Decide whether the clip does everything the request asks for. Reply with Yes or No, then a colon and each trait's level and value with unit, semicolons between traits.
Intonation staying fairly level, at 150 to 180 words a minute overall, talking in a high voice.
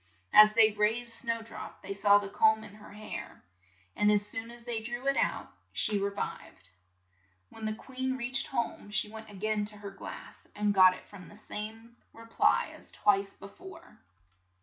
No: narrow, 2.2 semitones; average, 195 wpm; high, 215 Hz